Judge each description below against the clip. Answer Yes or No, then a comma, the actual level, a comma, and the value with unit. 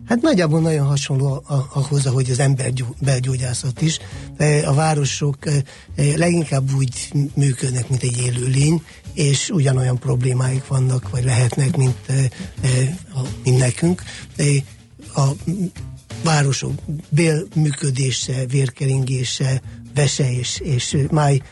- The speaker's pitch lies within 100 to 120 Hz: No, low, 135 Hz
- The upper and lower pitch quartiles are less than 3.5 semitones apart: Yes, narrow, 2.4 semitones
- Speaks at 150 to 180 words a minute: No, average, 110 wpm